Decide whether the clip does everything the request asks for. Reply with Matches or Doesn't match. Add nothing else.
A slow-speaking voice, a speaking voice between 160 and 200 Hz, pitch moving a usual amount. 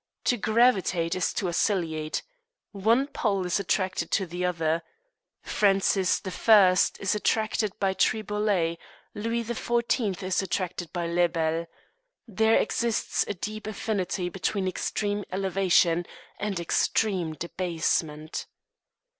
Matches